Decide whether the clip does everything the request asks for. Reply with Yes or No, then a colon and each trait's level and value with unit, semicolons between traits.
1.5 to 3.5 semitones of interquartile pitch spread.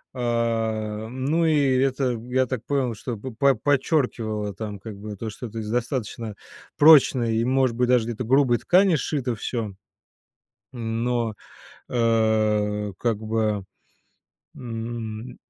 Yes: average, 2.9 semitones